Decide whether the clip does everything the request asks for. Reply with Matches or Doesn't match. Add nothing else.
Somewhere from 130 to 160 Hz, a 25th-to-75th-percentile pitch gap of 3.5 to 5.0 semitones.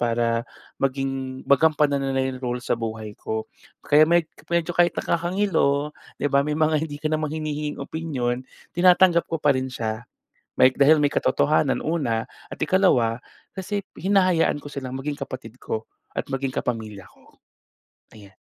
Matches